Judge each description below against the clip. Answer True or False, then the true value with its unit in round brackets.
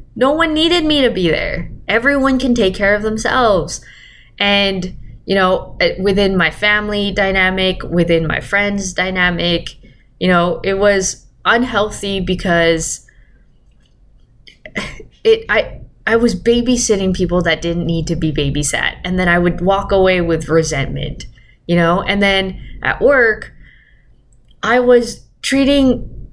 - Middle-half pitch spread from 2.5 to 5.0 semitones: True (4.1 semitones)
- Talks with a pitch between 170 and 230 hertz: True (190 Hz)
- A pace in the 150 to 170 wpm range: False (135 wpm)